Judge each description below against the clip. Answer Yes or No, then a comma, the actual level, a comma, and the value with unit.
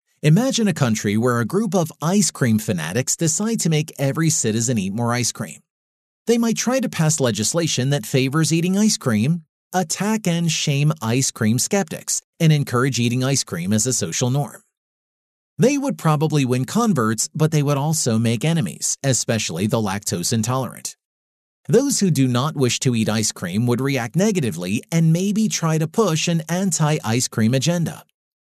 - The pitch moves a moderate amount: No, wide, 6.4 semitones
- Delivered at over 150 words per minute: Yes, average, 175 wpm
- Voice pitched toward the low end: No, medium, 150 Hz